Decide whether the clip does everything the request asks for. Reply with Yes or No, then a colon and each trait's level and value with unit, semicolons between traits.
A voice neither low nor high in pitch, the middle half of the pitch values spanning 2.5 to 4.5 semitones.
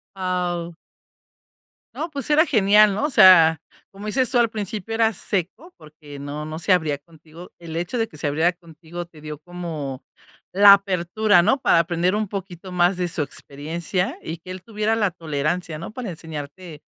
Yes: medium, 175 Hz; average, 4.2 semitones